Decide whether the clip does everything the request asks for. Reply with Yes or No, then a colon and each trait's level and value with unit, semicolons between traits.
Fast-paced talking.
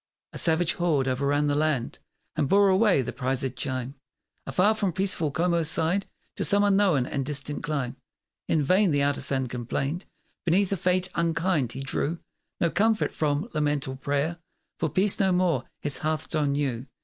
No: average, 165 wpm